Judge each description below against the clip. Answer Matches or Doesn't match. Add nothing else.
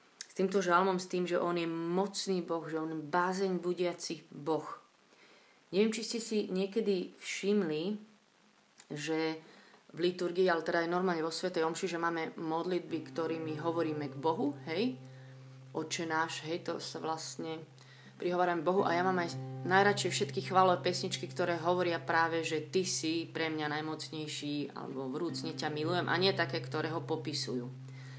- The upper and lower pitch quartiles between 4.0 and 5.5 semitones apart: Doesn't match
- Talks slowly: Doesn't match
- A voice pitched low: Doesn't match